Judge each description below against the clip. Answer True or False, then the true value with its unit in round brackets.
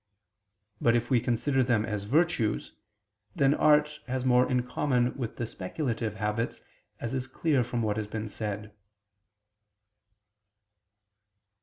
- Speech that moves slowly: True (130 wpm)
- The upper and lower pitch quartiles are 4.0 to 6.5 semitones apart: False (3.3 semitones)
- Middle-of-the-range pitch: False (120 Hz)